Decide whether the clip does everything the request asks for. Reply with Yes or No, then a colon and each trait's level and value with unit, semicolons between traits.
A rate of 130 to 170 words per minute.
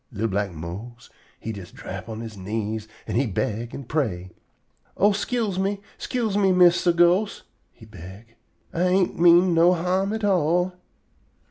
Yes: average, 155 wpm